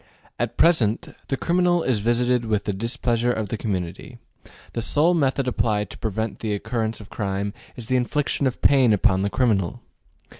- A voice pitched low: Yes, low, 115 Hz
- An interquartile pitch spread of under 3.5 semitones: No, average, 3.8 semitones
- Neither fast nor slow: Yes, average, 175 wpm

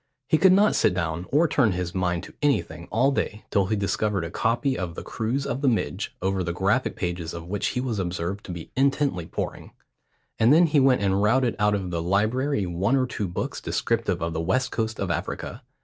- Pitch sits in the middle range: No, low, 105 Hz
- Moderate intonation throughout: No, wide, 6.5 semitones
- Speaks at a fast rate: Yes, fast, 220 wpm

